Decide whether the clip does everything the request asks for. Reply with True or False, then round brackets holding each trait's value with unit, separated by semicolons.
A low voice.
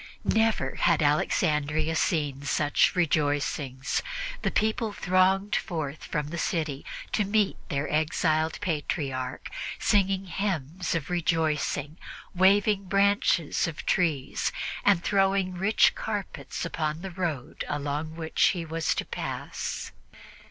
False (165 Hz)